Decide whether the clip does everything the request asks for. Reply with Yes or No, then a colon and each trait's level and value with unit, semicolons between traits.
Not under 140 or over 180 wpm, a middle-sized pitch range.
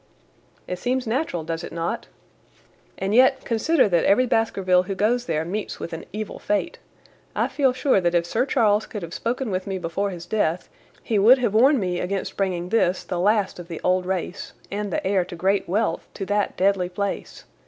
No: average, 200 wpm; average, 3.8 semitones